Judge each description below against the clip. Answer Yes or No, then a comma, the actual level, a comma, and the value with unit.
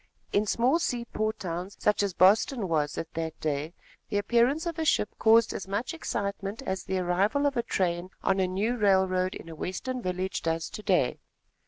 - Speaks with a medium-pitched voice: No, high, 195 Hz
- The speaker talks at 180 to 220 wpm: Yes, average, 190 wpm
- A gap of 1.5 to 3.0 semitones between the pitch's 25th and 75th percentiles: No, average, 4.3 semitones